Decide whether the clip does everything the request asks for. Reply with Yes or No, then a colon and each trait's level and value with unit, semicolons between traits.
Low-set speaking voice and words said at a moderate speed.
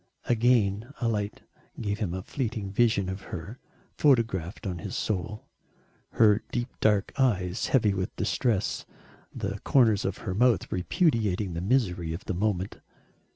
Yes: low, 105 Hz; average, 150 wpm